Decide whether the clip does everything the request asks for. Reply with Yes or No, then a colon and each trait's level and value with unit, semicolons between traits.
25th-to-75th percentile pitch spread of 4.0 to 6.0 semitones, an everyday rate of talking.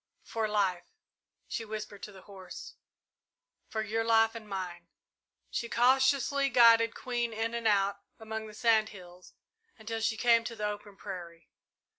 No: narrow, 2.4 semitones; average, 150 wpm